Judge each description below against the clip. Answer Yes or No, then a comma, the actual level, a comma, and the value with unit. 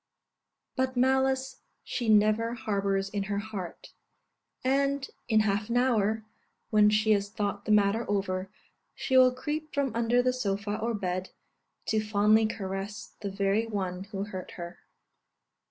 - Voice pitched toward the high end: Yes, high, 215 Hz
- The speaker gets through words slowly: No, average, 145 wpm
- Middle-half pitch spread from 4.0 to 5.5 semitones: No, average, 3.2 semitones